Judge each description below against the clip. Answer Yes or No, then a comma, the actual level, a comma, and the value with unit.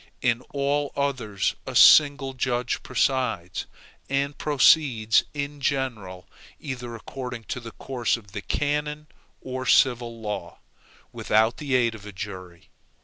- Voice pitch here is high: No, low, 125 Hz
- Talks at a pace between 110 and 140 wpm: Yes, slow, 135 wpm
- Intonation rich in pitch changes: No, average, 4.0 semitones